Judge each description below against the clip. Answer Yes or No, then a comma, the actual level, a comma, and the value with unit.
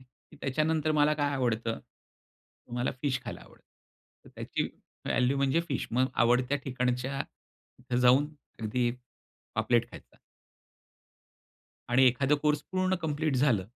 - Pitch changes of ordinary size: Yes, average, 3.1 semitones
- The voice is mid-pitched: No, low, 130 Hz